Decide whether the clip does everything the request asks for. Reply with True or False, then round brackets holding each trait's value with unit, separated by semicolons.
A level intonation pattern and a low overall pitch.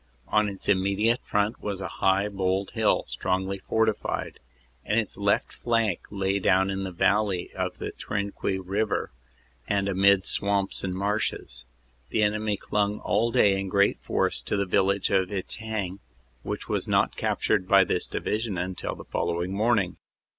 True (1.6 semitones; 100 Hz)